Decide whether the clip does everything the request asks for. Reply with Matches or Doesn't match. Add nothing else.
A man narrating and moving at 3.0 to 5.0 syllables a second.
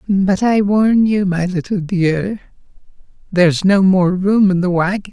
Matches